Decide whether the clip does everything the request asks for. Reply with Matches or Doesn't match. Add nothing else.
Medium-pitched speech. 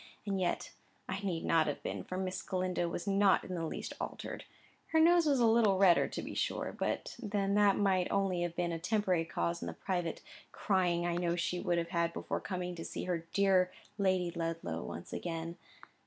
Matches